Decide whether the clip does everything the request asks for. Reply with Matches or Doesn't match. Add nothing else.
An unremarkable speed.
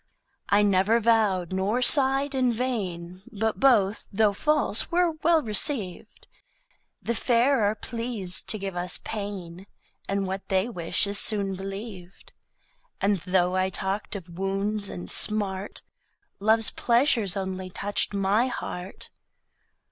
Doesn't match